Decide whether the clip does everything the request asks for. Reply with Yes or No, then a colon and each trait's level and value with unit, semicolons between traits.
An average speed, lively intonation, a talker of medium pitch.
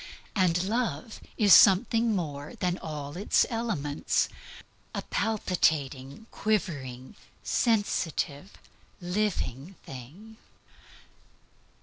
No: slow, 75 wpm; wide, 6.8 semitones; medium, 180 Hz